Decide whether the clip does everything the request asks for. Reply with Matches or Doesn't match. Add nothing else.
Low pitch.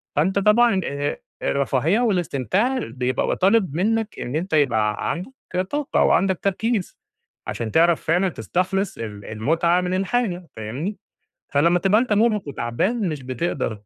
Doesn't match